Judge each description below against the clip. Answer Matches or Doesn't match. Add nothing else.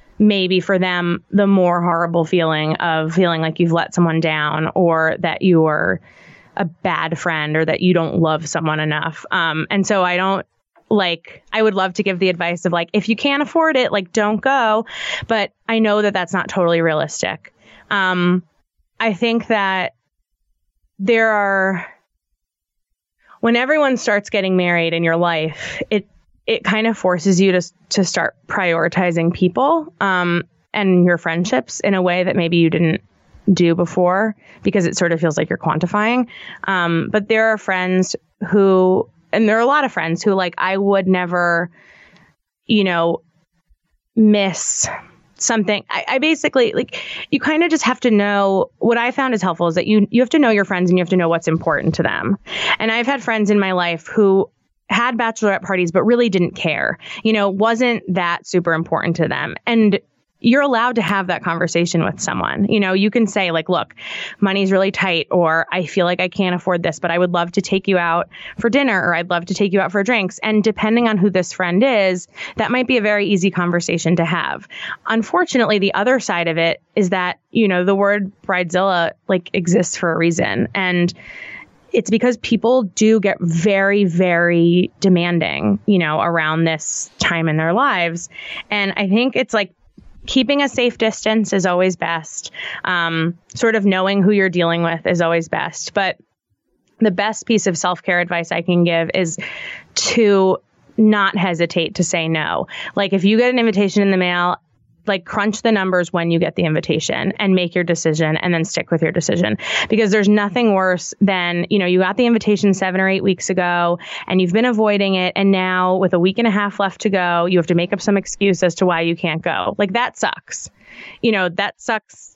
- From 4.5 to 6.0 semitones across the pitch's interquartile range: Doesn't match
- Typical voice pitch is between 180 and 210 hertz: Matches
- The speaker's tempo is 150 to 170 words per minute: Doesn't match